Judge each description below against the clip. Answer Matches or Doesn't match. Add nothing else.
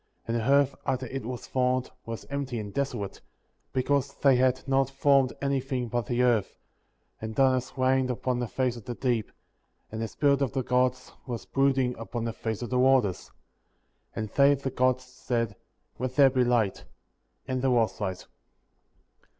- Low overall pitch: Matches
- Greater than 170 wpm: Matches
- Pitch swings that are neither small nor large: Doesn't match